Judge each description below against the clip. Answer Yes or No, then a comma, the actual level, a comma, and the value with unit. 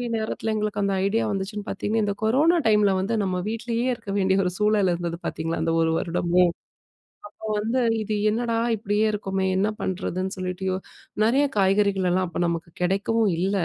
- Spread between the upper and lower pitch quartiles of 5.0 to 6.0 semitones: No, average, 2.8 semitones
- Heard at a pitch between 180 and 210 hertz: Yes, high, 200 Hz